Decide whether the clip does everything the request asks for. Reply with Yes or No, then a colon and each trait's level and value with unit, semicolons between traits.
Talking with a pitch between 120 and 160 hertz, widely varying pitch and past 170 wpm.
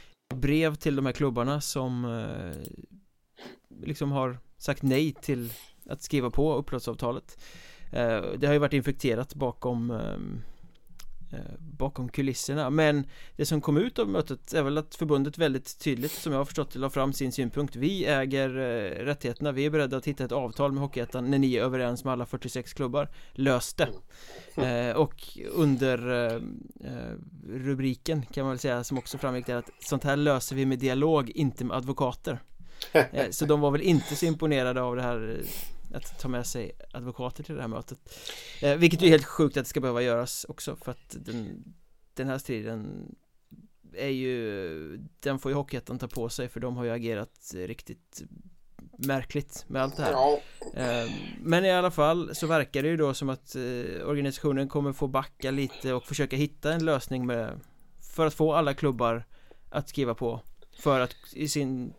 No: low, 135 Hz; average, 2.8 semitones; average, 180 wpm